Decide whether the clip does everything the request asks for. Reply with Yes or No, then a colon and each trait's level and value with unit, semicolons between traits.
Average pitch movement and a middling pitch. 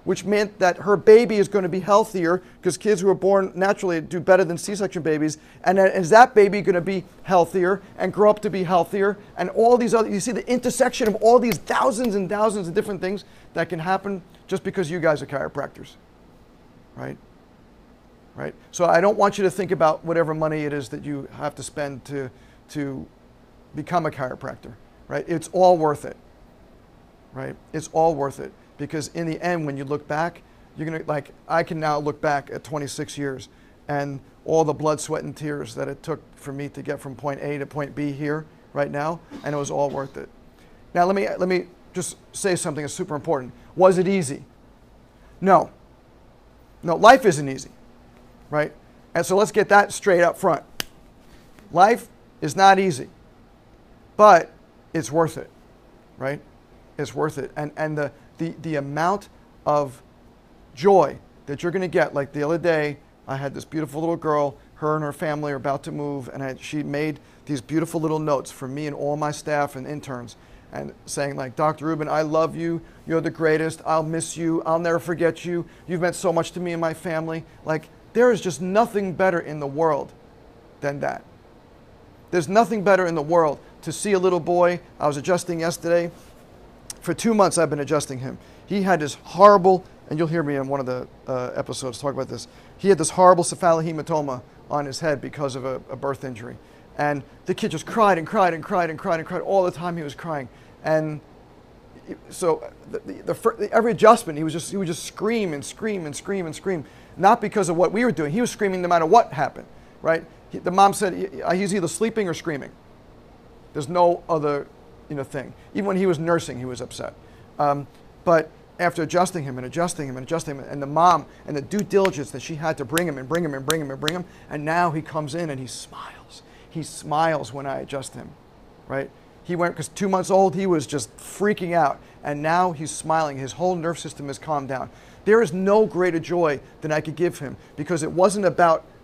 Yes: average, 4.2 semitones; medium, 160 Hz